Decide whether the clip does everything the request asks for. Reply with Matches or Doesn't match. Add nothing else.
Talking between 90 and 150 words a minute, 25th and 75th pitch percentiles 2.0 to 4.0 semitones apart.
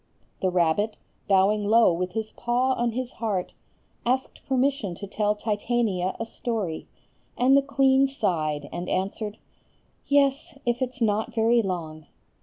Doesn't match